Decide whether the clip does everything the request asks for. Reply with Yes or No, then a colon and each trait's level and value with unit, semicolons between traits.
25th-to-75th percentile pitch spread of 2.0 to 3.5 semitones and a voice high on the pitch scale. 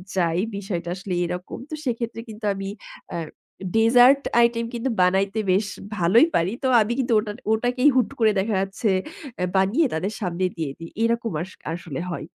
No: average, 4.4 semitones; high, 210 Hz